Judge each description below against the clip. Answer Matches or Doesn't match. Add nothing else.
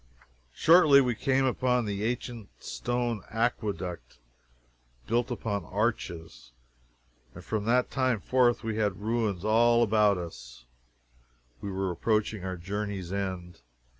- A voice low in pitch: Matches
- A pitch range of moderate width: Matches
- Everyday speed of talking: Doesn't match